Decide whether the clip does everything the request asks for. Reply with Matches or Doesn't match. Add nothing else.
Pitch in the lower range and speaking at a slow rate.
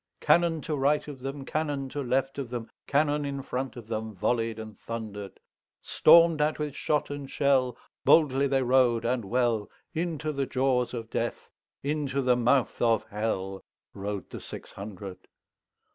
Matches